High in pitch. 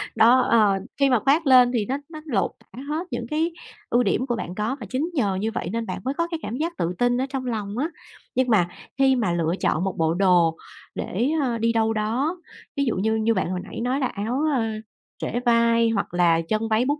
Yes: high, 230 Hz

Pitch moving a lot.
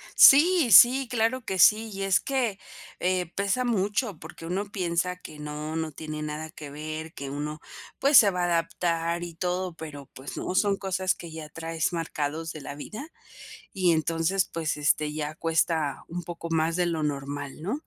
No: average, 3.9 semitones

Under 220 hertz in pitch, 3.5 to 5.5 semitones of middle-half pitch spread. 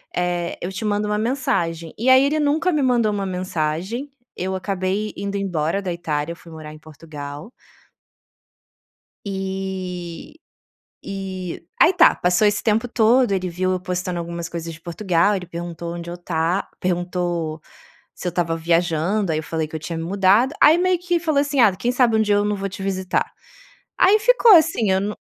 Yes: medium, 185 Hz; average, 4.1 semitones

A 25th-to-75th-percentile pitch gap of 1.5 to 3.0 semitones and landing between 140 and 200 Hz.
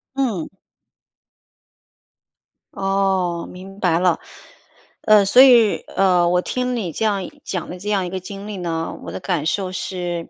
Yes: narrow, 2.5 semitones; high, 190 Hz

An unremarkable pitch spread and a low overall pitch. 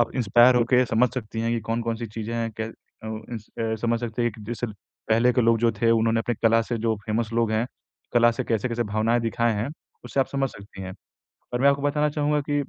No: narrow, 1.5 semitones; low, 115 Hz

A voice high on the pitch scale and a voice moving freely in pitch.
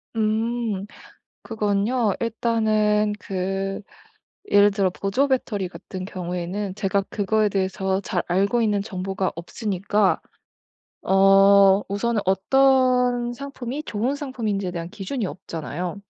No: high, 205 Hz; average, 3.2 semitones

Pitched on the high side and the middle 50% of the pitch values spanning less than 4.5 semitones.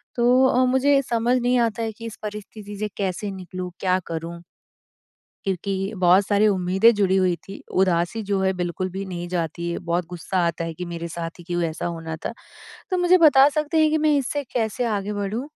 No: high, 195 Hz; average, 4.8 semitones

